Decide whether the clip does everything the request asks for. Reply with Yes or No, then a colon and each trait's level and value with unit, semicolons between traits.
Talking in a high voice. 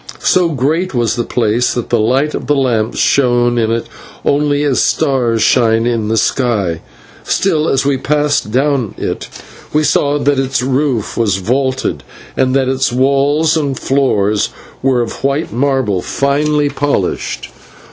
No: low, 130 Hz